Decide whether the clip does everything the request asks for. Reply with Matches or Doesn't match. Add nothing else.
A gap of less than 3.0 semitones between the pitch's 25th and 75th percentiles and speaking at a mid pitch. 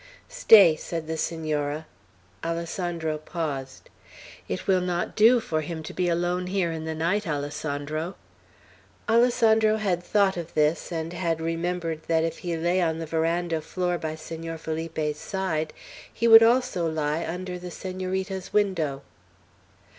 Matches